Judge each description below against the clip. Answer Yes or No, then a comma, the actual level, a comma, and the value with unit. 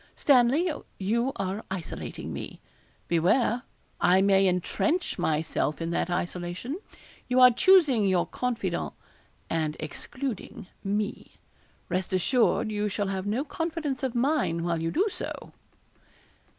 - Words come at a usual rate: No, slow, 125 wpm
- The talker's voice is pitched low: No, high, 205 Hz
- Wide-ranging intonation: Yes, wide, 6.4 semitones